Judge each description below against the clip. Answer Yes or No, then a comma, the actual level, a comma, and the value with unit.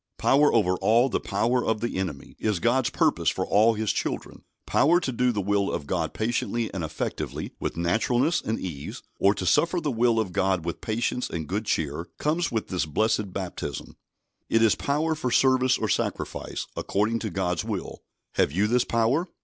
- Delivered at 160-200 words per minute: Yes, average, 190 wpm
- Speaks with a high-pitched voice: No, low, 110 Hz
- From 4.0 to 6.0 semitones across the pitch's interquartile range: Yes, average, 5.0 semitones